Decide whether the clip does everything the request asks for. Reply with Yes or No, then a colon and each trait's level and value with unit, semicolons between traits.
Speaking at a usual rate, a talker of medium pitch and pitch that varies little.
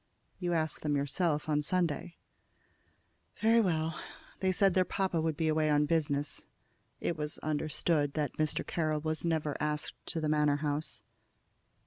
Yes: average, 150 wpm; medium, 155 Hz; narrow, 2.0 semitones